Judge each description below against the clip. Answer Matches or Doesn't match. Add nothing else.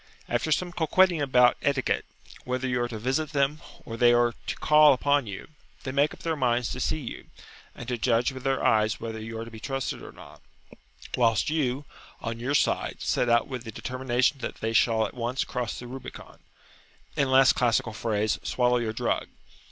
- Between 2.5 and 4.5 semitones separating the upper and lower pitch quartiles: Matches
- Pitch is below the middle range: Matches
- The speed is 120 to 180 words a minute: Doesn't match